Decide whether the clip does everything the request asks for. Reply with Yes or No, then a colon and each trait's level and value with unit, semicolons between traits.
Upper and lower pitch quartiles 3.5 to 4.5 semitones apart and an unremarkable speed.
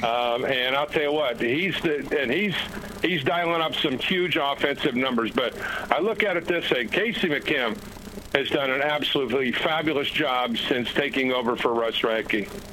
Yes: average, 4.1 semitones; average, 180 wpm